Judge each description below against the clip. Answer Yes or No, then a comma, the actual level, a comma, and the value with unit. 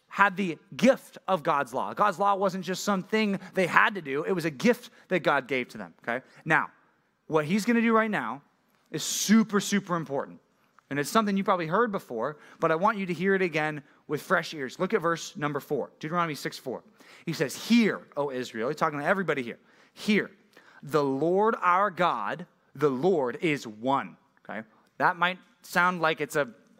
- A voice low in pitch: No, medium, 185 Hz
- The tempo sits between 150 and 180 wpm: No, average, 195 wpm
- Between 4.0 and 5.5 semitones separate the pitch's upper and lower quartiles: Yes, average, 4.9 semitones